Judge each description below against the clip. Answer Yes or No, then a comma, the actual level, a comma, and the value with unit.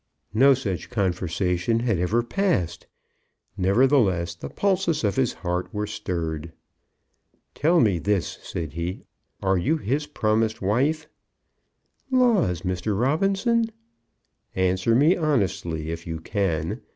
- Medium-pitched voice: No, low, 105 Hz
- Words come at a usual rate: No, slow, 115 wpm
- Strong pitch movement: Yes, wide, 7.8 semitones